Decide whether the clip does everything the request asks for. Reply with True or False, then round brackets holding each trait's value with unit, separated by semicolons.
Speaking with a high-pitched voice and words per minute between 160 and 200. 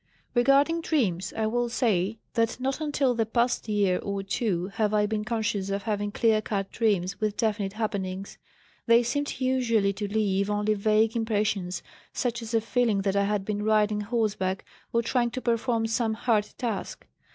True (215 Hz; 175 wpm)